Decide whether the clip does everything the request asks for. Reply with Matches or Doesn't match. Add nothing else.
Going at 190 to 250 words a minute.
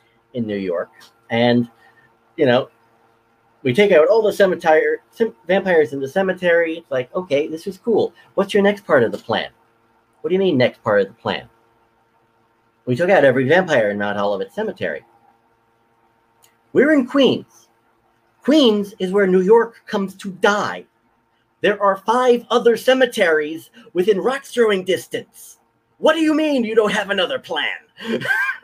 Doesn't match